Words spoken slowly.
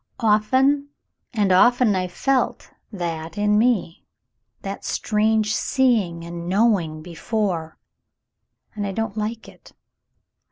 Yes: slow, 115 wpm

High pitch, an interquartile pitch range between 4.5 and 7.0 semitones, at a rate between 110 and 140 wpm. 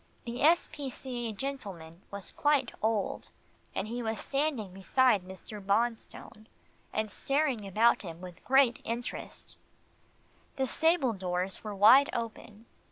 Yes: high, 225 Hz; average, 4.9 semitones; slow, 135 wpm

